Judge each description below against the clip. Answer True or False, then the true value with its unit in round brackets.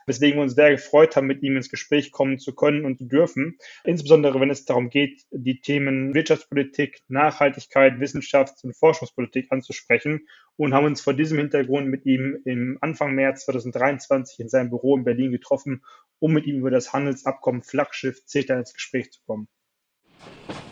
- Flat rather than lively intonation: True (1.7 semitones)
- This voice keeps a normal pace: True (170 wpm)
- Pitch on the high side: False (135 Hz)